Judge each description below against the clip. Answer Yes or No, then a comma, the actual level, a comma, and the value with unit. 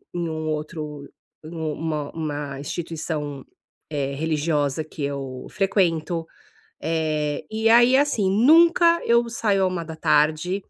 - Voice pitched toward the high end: No, medium, 160 Hz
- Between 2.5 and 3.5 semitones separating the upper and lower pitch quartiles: No, average, 4.5 semitones